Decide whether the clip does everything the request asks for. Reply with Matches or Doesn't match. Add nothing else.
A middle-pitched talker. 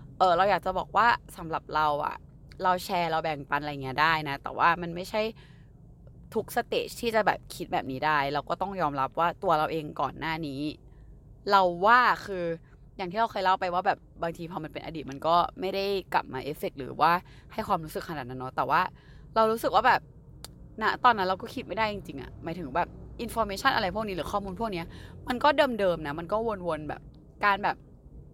Matches